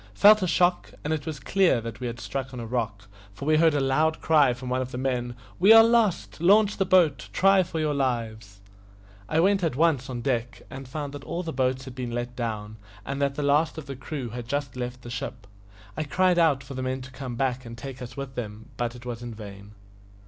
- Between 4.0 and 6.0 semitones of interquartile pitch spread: Yes, average, 4.4 semitones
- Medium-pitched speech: No, low, 130 Hz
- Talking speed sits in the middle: No, fast, 245 wpm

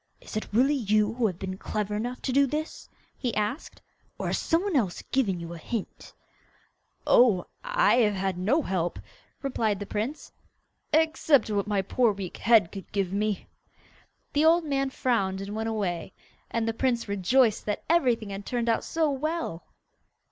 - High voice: Yes, high, 225 Hz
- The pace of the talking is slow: No, average, 175 wpm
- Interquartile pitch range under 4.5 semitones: No, average, 5.2 semitones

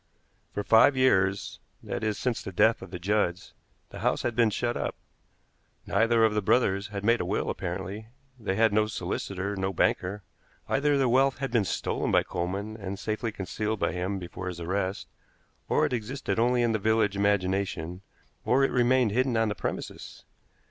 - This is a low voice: Yes, low, 105 Hz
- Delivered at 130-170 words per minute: No, average, 185 wpm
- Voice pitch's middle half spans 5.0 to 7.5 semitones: No, average, 3.4 semitones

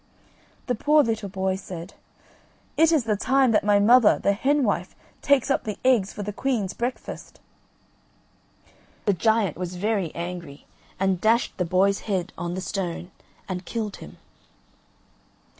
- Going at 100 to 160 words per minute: Yes, average, 150 wpm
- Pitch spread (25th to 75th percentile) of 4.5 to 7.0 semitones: No, average, 4.0 semitones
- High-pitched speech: Yes, high, 205 Hz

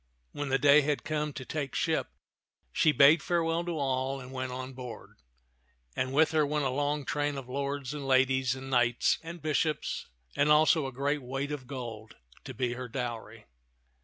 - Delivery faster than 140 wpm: Yes, average, 185 wpm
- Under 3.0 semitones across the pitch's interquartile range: Yes, narrow, 2.5 semitones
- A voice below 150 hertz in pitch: Yes, low, 135 Hz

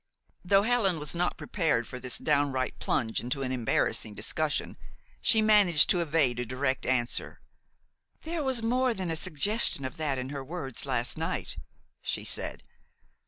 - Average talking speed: Yes, average, 160 wpm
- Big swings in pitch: Yes, wide, 6.9 semitones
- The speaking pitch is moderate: Yes, medium, 150 Hz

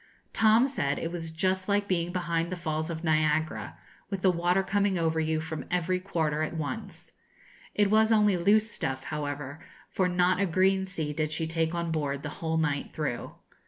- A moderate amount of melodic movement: Yes, average, 3.2 semitones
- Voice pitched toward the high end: No, medium, 170 Hz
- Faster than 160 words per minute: Yes, average, 190 wpm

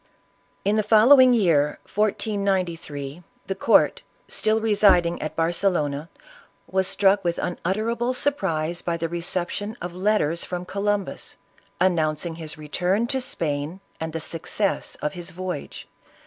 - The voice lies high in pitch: No, medium, 180 Hz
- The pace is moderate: No, slow, 125 wpm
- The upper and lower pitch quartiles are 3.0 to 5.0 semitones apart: Yes, average, 4.0 semitones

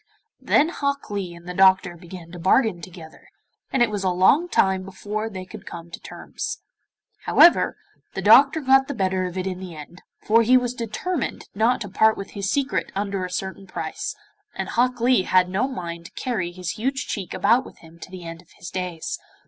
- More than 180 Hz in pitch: Yes, high, 190 Hz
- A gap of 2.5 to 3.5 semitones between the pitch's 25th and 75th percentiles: No, average, 5.0 semitones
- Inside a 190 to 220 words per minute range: Yes, fast, 205 wpm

